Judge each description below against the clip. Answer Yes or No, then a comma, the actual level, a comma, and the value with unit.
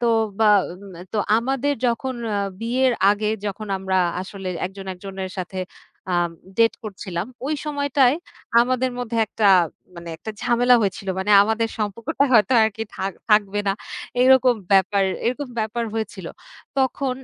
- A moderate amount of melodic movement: Yes, average, 4.2 semitones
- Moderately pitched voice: No, high, 220 Hz